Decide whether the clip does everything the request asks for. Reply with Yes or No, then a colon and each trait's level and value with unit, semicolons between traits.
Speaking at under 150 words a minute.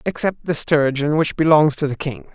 No: fast, 205 wpm